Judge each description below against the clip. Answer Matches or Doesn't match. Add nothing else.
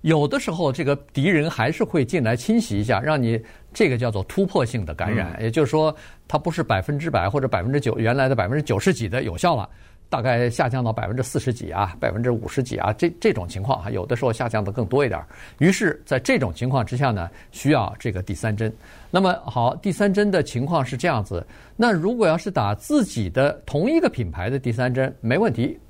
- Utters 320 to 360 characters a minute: Matches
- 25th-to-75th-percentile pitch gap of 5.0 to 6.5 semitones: Matches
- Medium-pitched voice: Doesn't match